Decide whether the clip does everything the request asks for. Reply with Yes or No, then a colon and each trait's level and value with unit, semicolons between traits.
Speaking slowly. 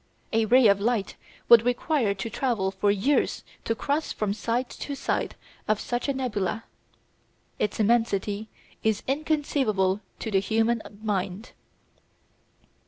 Yes: slow, 130 wpm